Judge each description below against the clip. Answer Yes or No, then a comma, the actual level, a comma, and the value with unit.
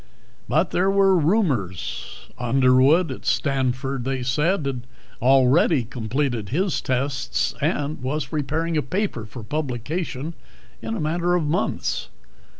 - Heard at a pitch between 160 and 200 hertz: No, medium, 140 Hz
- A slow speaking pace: Yes, slow, 125 wpm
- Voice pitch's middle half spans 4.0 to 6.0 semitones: Yes, average, 4.5 semitones